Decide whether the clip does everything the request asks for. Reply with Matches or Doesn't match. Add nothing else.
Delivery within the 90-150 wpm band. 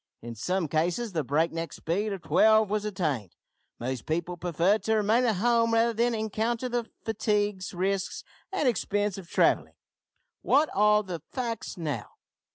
Doesn't match